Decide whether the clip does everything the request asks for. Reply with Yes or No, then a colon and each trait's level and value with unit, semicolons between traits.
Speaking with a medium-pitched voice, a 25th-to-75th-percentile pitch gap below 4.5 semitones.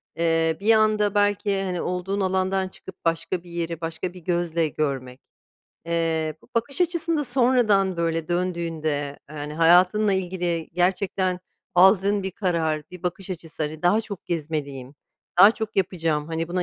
Yes: medium, 180 Hz; average, 3.1 semitones